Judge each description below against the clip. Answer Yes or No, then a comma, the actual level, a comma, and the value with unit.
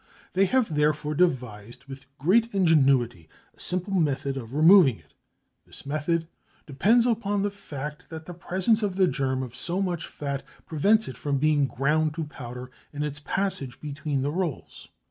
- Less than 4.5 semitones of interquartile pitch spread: No, average, 5.1 semitones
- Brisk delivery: No, average, 165 wpm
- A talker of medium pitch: Yes, medium, 150 Hz